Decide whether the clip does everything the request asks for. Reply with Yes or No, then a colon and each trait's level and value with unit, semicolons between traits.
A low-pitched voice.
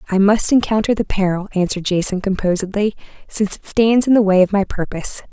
No: high, 200 Hz